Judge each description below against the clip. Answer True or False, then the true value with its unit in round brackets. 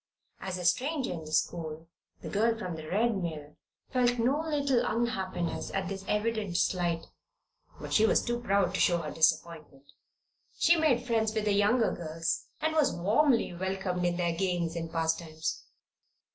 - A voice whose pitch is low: False (190 Hz)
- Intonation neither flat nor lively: False (5.7 semitones)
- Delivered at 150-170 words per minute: True (165 wpm)